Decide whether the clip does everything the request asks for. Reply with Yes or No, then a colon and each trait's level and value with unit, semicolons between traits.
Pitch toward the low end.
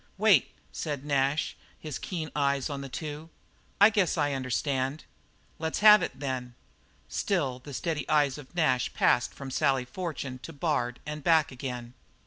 No: medium, 145 Hz